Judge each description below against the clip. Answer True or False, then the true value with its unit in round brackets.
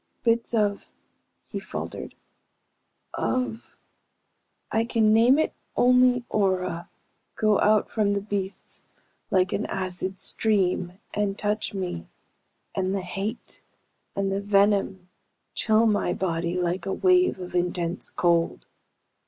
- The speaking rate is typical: False (120 wpm)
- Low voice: False (200 Hz)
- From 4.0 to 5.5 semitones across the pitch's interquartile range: False (3.0 semitones)